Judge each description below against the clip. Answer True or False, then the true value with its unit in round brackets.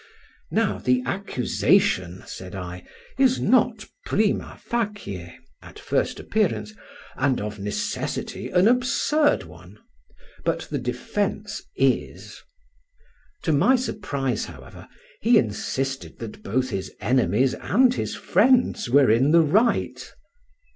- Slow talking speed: True (105 wpm)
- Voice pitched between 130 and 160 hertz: True (135 Hz)